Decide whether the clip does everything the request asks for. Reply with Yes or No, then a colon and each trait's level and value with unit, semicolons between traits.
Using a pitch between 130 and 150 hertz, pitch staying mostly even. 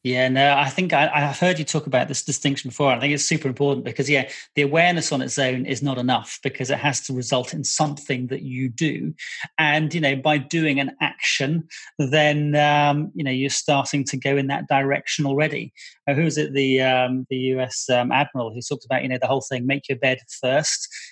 Yes: medium, 140 Hz; narrow, 2.1 semitones